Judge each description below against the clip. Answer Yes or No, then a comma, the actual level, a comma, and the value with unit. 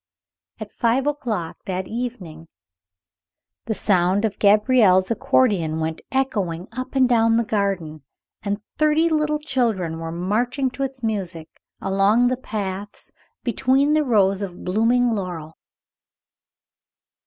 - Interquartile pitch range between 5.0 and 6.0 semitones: Yes, wide, 5.4 semitones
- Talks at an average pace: No, slow, 120 wpm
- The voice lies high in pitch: Yes, high, 215 Hz